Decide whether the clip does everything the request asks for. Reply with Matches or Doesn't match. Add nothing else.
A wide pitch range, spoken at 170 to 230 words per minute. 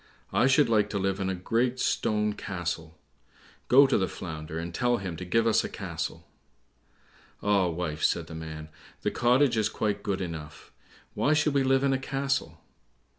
Matches